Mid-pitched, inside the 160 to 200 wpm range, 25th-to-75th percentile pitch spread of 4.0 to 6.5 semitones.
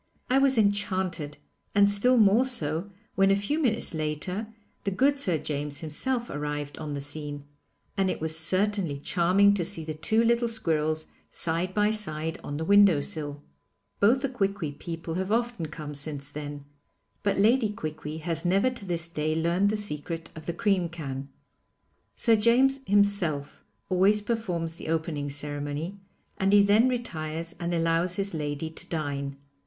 Yes: medium, 170 Hz; average, 165 wpm; average, 4.9 semitones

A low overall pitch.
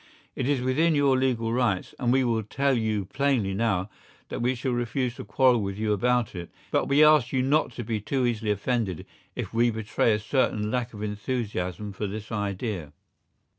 Yes: low, 115 Hz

